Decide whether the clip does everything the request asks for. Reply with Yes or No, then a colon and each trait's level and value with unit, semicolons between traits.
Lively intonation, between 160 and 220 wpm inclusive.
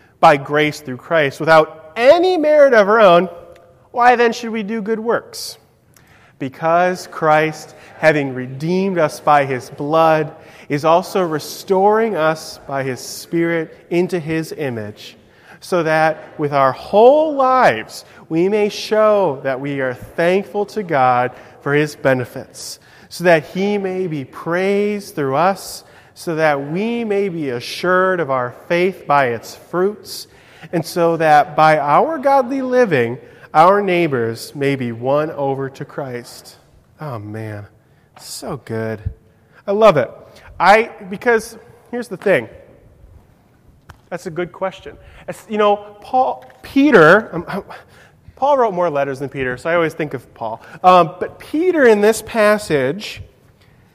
No: wide, 6.4 semitones; average, 140 wpm